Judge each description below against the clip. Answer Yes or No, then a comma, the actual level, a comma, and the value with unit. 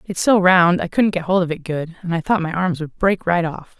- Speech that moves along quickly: Yes, fast, 300 wpm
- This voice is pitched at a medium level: Yes, medium, 175 Hz